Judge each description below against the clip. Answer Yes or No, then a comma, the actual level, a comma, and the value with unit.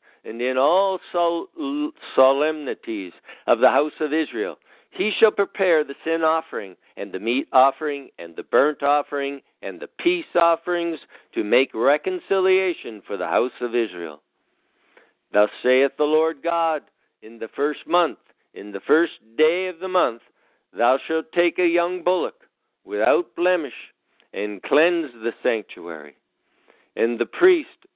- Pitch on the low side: No, medium, 160 Hz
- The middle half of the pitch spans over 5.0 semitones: Yes, wide, 5.4 semitones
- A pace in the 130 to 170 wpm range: Yes, average, 140 wpm